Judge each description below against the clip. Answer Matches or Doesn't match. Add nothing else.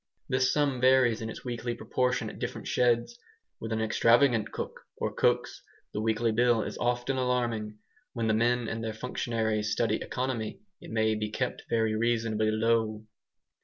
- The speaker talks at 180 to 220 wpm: Doesn't match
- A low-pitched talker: Matches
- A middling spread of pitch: Doesn't match